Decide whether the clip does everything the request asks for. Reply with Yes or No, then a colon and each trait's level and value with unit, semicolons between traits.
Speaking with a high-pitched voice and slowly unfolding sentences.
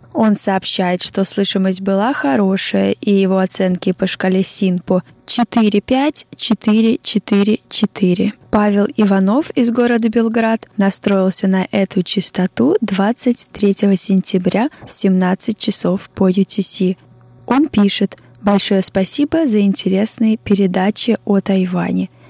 Yes: high, 200 Hz; slow, 100 wpm